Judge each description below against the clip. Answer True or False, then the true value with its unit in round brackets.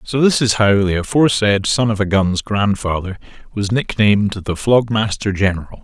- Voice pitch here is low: True (105 Hz)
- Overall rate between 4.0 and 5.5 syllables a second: True (5.0 syllables/s)